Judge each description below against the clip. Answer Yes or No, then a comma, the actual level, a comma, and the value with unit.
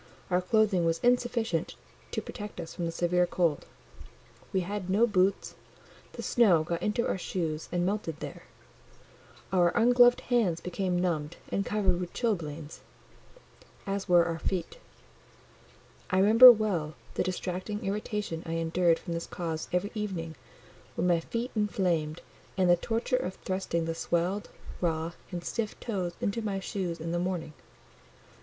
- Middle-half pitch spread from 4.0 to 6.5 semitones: No, average, 3.6 semitones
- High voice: No, medium, 180 Hz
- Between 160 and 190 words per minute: No, average, 150 wpm